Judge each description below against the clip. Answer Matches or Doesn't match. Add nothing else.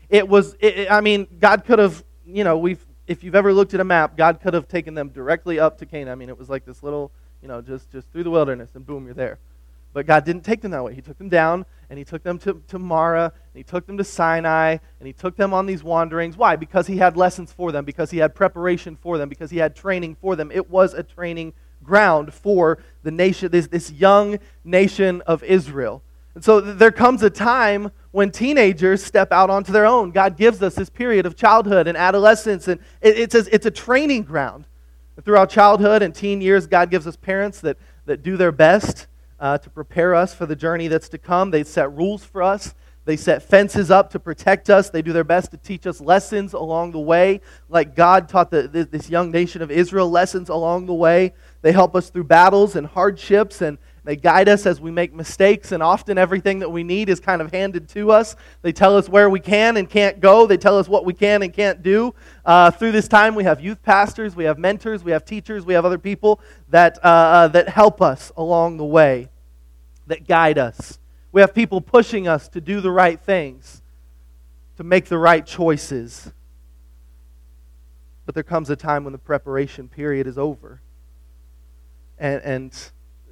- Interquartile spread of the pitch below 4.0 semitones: Doesn't match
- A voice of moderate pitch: Matches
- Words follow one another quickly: Matches